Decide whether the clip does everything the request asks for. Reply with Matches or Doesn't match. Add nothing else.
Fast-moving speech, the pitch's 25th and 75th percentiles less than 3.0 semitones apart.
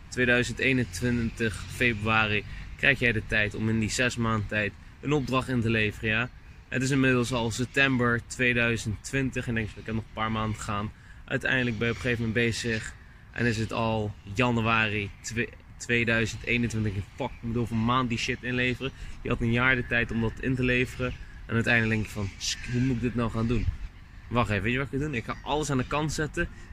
Matches